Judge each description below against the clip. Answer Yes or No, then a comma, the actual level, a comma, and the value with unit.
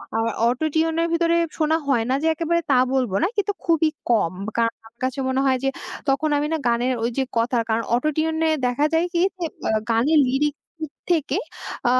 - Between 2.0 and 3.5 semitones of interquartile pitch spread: No, average, 4.9 semitones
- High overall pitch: Yes, very high, 285 Hz